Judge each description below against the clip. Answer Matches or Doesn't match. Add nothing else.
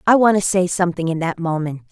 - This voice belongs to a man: Doesn't match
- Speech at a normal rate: Doesn't match